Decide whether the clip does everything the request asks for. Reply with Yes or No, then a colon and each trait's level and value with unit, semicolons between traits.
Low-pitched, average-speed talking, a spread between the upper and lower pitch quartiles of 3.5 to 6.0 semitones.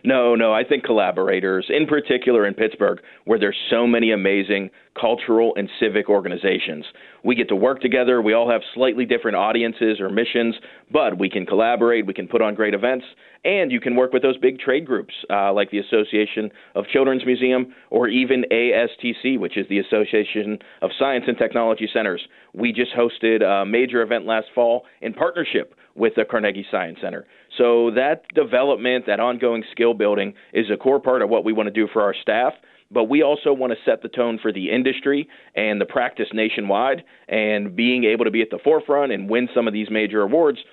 No: low, 115 Hz; average, 195 wpm; average, 2.9 semitones